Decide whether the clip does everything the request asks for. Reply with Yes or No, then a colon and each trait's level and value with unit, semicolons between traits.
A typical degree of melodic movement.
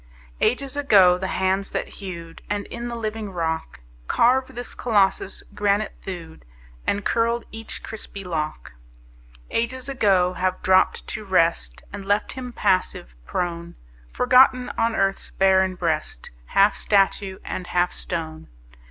Yes: average, 4.1 semitones